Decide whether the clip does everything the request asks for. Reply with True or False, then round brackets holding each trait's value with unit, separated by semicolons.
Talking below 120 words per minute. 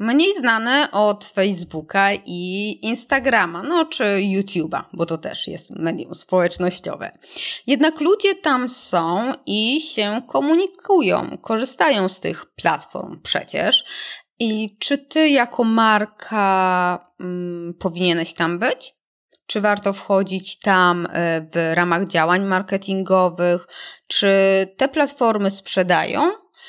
True (110 wpm)